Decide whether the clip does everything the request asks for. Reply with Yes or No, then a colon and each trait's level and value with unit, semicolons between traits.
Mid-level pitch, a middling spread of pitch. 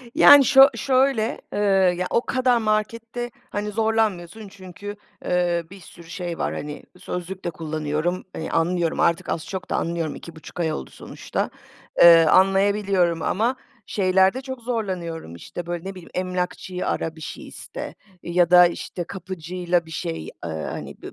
Yes: medium, 180 Hz; average, 3.5 semitones